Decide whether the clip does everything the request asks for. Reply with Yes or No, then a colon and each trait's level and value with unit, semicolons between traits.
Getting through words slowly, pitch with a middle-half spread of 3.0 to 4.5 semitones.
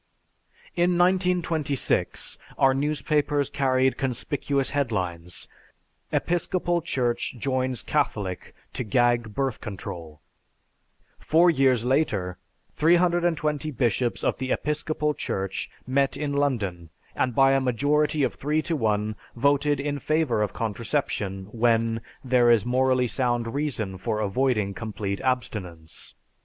No: slow, 115 wpm; average, 5.2 semitones